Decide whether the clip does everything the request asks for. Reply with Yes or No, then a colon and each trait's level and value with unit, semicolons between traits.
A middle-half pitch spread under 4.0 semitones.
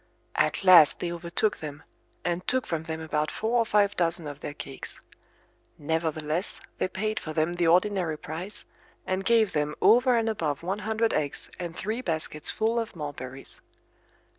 No: average, 5.2 semitones